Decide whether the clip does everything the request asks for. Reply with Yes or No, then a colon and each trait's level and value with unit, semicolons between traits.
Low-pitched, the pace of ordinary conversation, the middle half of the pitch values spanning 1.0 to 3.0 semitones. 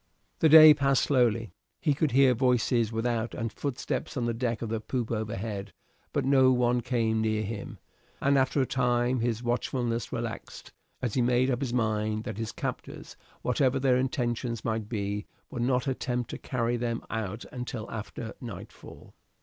Yes: low, 120 Hz; average, 170 wpm; narrow, 2.4 semitones